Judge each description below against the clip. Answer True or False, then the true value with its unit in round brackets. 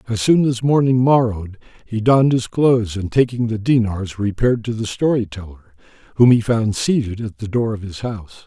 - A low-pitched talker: True (115 Hz)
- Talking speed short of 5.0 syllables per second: False (5.6 syllables/s)